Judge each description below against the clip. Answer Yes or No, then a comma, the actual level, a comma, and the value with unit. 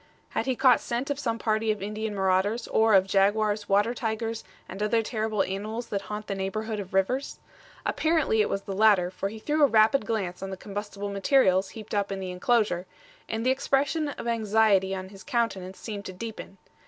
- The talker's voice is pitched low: No, high, 215 Hz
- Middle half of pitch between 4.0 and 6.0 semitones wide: No, average, 2.8 semitones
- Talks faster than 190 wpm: Yes, average, 200 wpm